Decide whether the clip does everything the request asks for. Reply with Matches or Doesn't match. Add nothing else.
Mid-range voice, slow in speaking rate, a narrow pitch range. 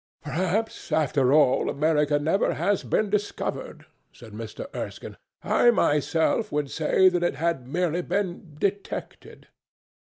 Doesn't match